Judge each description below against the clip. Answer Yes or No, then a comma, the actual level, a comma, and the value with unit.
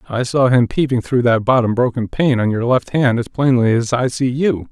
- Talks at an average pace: No, fast, 240 wpm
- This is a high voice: No, low, 125 Hz